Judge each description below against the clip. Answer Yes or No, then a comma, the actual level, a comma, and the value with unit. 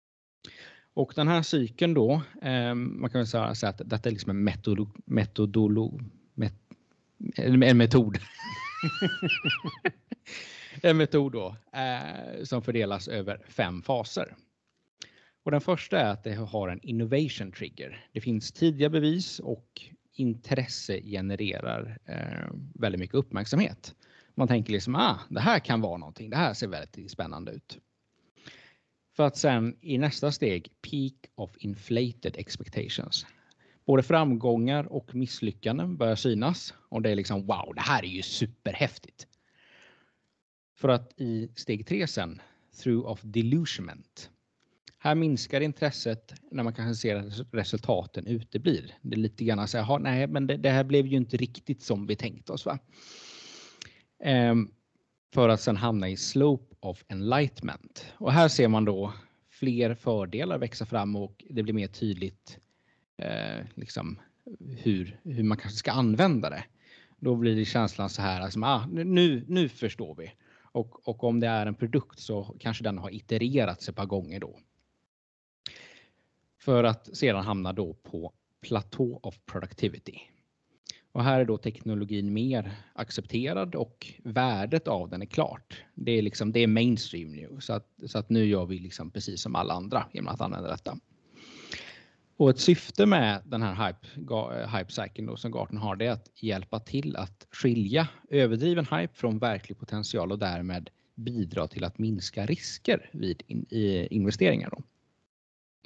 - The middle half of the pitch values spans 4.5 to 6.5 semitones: No, average, 4.1 semitones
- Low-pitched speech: Yes, low, 115 Hz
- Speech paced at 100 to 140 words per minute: No, average, 150 wpm